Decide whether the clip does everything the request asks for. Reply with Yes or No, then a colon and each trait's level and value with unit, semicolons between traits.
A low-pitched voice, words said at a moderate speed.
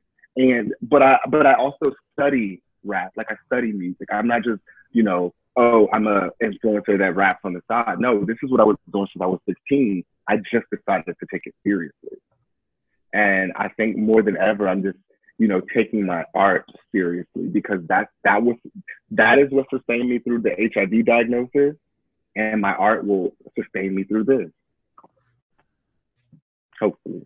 Yes: low, 110 Hz; average, 175 wpm